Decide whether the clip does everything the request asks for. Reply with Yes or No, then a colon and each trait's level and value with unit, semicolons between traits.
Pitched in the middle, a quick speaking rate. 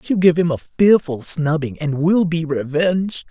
No: medium, 160 Hz; average, 180 wpm